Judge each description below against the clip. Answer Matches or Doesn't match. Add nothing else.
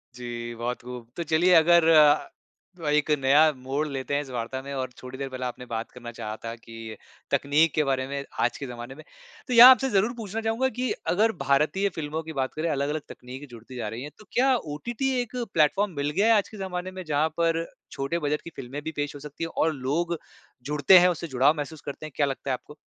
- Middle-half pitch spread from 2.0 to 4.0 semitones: Doesn't match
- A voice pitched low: Doesn't match